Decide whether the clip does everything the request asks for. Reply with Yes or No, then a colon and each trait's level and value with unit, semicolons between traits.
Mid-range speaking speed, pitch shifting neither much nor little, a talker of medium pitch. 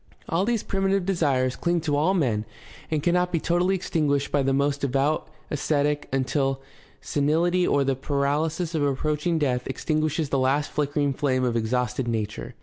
Yes: average, 165 wpm; average, 3.4 semitones; medium, 145 Hz